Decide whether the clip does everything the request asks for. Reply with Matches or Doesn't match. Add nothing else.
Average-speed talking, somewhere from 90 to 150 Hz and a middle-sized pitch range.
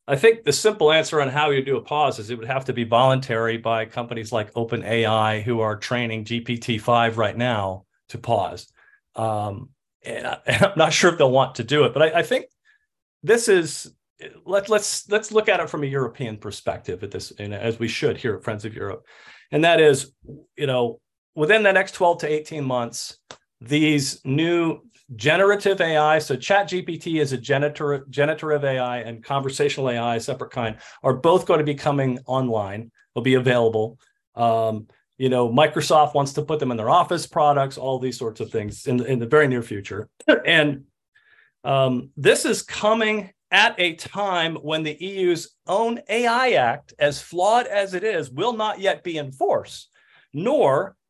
Doesn't match